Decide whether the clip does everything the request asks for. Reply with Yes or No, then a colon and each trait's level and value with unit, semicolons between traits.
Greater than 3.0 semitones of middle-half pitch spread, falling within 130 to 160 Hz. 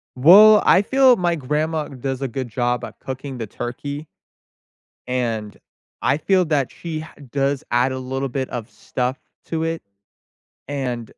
Yes: average, 4.0 semitones; low, 135 Hz